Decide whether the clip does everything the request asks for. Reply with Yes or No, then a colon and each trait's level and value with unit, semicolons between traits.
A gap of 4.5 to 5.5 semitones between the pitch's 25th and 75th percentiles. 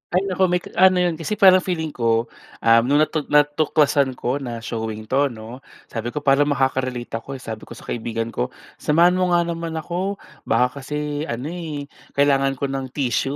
Yes: average, 4.8 semitones